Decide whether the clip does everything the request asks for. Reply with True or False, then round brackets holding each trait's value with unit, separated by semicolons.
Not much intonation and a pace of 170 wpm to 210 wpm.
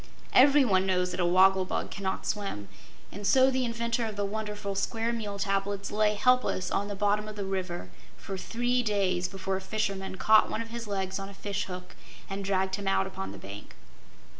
True (2.2 semitones; 190 wpm)